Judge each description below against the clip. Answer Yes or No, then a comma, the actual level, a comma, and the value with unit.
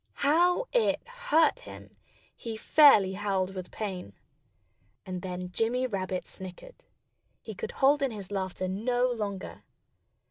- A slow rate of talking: Yes, slow, 130 wpm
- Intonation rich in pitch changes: Yes, wide, 7.4 semitones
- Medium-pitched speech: No, high, 215 Hz